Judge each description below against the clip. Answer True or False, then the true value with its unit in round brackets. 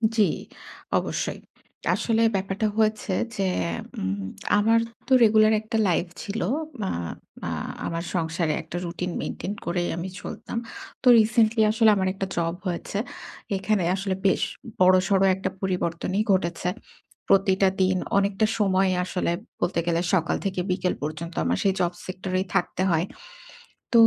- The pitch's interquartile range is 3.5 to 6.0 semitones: False (2.8 semitones)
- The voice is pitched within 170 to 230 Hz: True (190 Hz)